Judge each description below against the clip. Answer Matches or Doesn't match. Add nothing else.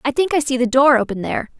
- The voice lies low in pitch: Doesn't match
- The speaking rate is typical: Doesn't match